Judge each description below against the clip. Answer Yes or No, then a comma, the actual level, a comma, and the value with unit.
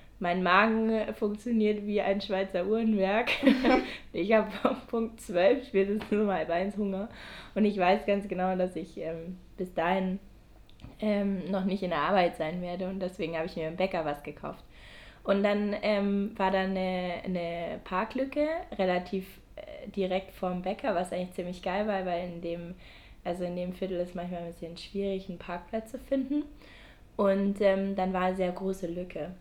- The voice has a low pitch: No, high, 190 Hz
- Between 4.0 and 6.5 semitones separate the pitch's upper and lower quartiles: No, average, 2.7 semitones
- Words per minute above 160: Yes, average, 170 wpm